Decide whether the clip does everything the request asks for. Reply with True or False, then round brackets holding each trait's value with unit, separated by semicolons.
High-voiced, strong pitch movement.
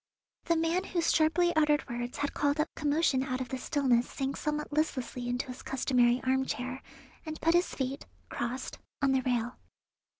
False (270 Hz; 3.6 semitones)